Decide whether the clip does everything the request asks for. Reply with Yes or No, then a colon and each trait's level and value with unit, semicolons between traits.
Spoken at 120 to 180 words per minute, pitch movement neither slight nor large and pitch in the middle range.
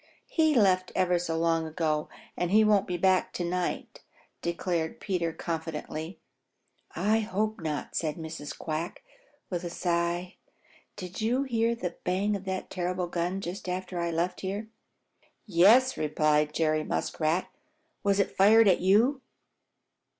Yes: average, 145 wpm; average, 3.2 semitones; medium, 180 Hz